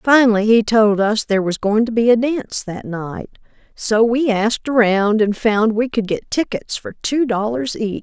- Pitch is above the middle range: Yes, high, 225 Hz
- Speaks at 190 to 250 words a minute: Yes, average, 200 wpm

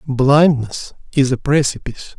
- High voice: No, low, 135 Hz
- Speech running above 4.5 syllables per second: No, 4.4 syllables/s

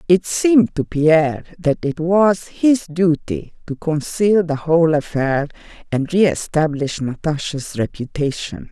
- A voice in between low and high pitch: Yes, medium, 160 Hz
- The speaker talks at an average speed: No, slow, 125 wpm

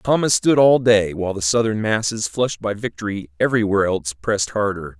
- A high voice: No, low, 105 Hz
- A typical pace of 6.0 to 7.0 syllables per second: Yes, 6.1 syllables/s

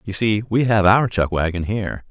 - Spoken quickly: Yes, fast, 230 wpm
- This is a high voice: No, low, 100 Hz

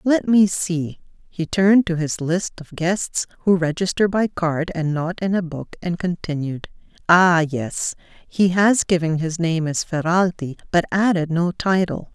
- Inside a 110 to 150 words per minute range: No, average, 170 wpm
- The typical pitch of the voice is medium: Yes, medium, 175 Hz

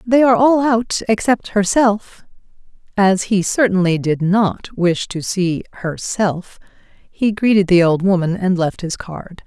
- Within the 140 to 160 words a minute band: Yes, average, 145 wpm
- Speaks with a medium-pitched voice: No, high, 200 Hz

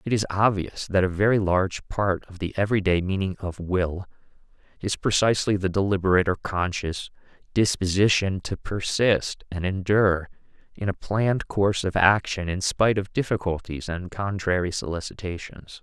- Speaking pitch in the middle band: No, very low, 95 Hz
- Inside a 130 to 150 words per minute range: Yes, average, 145 wpm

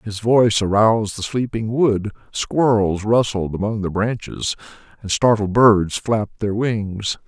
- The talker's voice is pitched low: Yes, low, 110 Hz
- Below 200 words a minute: Yes, average, 140 wpm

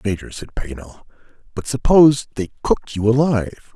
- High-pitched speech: No, low, 115 Hz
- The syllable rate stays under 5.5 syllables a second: No, 6.0 syllables/s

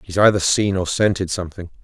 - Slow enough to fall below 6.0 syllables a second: No, 6.1 syllables/s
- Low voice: Yes, very low, 95 Hz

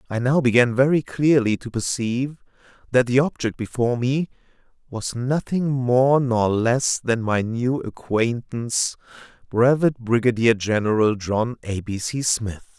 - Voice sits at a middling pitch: No, low, 120 Hz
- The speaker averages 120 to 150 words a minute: Yes, slow, 135 wpm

